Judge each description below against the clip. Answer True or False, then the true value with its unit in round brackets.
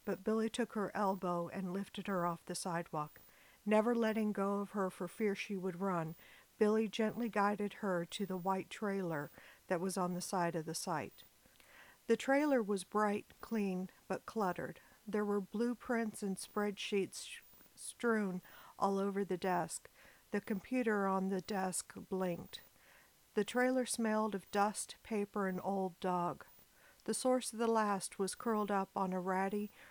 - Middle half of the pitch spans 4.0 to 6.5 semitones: False (2.6 semitones)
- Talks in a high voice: True (200 Hz)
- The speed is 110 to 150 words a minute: False (160 wpm)